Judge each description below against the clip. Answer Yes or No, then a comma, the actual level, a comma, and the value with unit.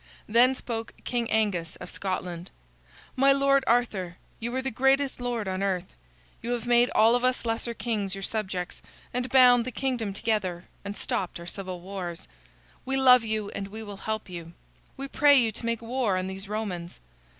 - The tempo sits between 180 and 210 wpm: Yes, average, 185 wpm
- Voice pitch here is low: No, high, 220 Hz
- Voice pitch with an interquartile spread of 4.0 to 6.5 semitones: Yes, average, 4.4 semitones